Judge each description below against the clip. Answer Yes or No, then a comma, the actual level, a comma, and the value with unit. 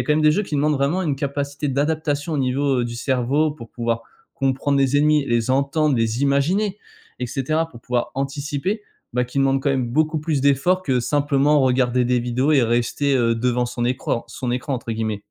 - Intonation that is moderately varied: Yes, average, 3.2 semitones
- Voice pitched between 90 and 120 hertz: No, low, 135 Hz